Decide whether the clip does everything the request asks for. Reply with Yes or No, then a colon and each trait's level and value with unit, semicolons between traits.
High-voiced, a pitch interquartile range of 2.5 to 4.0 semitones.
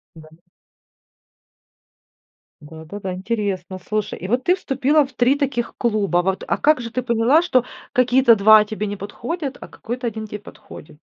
No: high, 225 Hz; average, 4.4 semitones